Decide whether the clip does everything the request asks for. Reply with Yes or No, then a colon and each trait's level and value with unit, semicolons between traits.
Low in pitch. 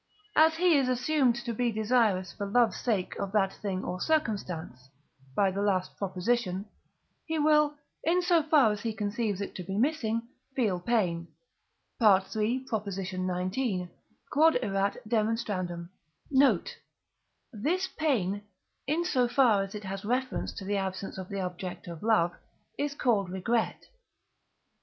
No: high, 215 Hz